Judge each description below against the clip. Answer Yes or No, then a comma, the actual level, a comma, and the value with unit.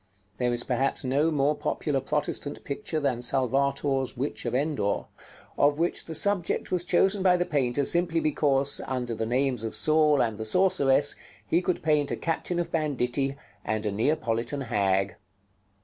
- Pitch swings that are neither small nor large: Yes, average, 4.3 semitones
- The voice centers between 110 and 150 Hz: Yes, medium, 140 Hz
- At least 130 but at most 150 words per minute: No, average, 165 wpm